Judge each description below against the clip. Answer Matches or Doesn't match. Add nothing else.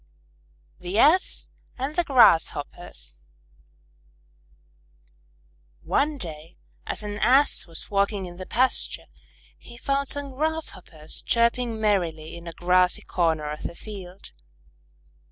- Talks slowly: Matches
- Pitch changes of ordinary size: Doesn't match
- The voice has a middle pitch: Doesn't match